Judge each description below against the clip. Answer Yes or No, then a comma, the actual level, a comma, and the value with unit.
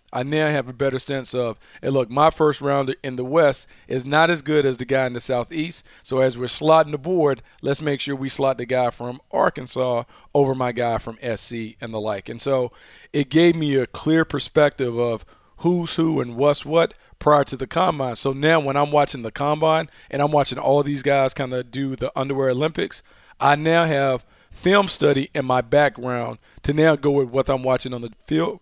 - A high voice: No, low, 135 Hz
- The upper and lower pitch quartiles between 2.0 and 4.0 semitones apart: Yes, average, 2.8 semitones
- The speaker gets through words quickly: Yes, fast, 215 wpm